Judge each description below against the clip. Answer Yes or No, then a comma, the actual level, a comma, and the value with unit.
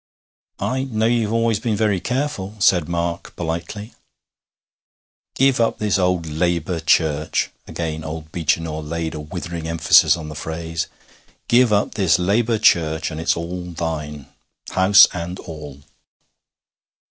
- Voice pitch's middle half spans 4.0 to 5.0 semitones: Yes, average, 4.6 semitones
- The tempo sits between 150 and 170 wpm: No, slow, 135 wpm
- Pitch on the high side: No, very low, 85 Hz